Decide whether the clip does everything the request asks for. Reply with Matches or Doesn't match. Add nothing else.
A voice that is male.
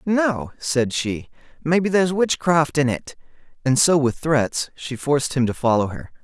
Matches